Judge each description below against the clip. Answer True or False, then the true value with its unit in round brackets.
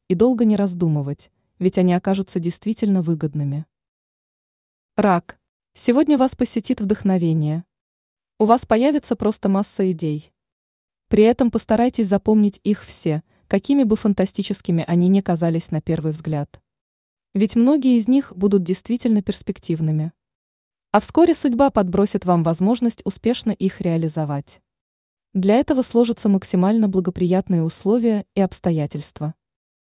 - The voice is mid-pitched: False (200 Hz)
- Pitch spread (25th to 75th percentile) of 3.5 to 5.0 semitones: True (4.7 semitones)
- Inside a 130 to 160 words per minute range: False (120 wpm)